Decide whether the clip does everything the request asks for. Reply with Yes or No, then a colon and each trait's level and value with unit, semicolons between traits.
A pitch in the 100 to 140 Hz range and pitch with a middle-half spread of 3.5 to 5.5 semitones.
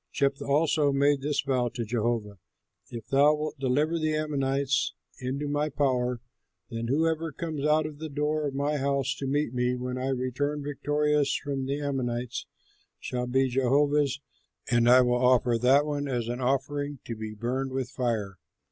No: low, 135 Hz; average, 2.8 semitones